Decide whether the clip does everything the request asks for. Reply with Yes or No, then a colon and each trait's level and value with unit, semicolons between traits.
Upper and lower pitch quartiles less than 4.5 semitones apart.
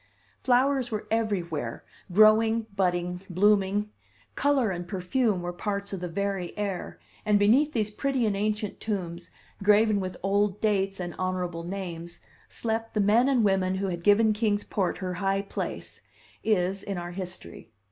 Yes: average, 2.9 semitones